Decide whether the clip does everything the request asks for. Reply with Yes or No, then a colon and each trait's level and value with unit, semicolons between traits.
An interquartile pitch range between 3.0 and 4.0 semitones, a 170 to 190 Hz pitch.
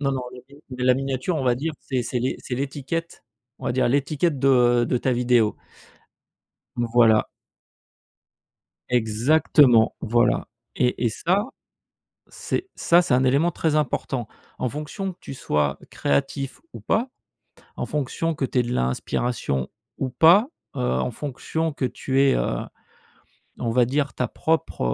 No: average, 3.7 semitones; low, 130 Hz